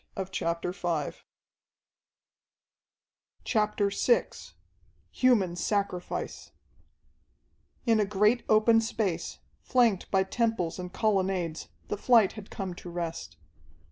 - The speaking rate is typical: No, slow, 85 wpm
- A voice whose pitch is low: No, high, 190 Hz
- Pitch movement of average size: Yes, average, 4.1 semitones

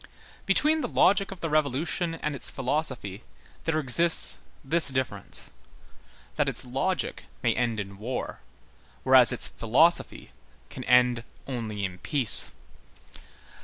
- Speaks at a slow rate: Yes, slow, 120 wpm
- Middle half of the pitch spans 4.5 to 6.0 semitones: Yes, wide, 5.6 semitones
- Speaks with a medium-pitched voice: No, low, 130 Hz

